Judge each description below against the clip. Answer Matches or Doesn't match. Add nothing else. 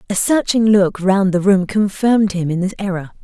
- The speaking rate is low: Doesn't match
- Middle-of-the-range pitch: Doesn't match